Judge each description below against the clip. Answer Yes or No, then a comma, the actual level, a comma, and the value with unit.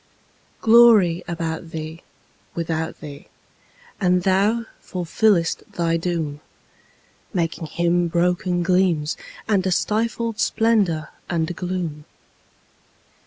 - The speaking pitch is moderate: Yes, medium, 175 Hz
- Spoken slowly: Yes, slow, 85 wpm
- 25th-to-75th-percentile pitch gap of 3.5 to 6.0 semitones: No, average, 2.7 semitones